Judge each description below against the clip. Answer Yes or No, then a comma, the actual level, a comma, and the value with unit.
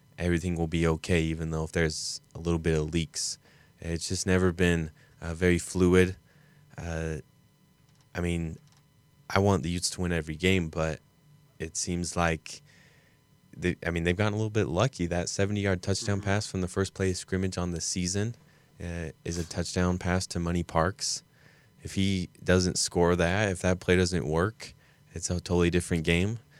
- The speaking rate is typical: Yes, average, 185 wpm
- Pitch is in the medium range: No, very low, 90 Hz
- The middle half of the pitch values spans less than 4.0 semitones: Yes, narrow, 2.6 semitones